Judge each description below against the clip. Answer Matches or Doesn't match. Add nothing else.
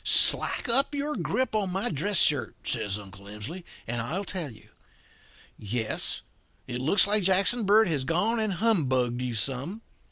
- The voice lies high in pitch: Doesn't match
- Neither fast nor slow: Matches